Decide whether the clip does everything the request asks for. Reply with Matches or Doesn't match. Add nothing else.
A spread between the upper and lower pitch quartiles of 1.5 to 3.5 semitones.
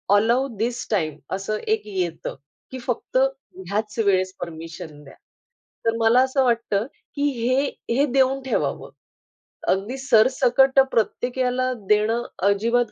Doesn't match